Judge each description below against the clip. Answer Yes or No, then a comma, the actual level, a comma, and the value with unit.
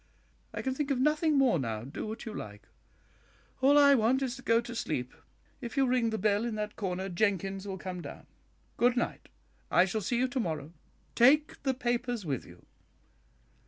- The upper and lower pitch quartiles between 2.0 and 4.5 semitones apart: No, wide, 5.6 semitones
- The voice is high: Yes, high, 230 Hz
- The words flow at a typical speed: Yes, average, 195 wpm